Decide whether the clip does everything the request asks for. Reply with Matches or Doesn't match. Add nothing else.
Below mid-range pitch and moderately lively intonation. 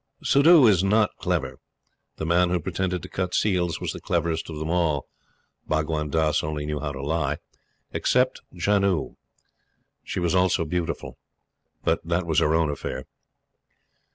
Matches